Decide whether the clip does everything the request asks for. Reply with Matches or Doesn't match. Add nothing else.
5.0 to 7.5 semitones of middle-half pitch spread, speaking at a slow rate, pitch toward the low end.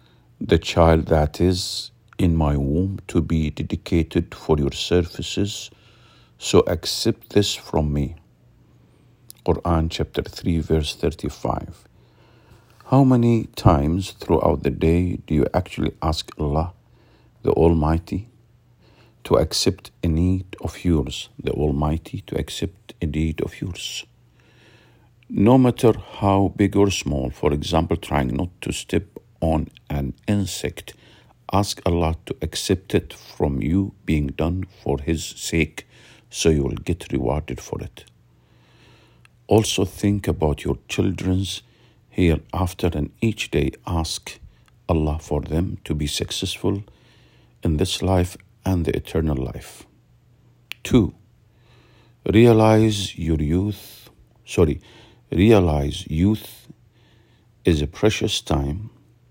Matches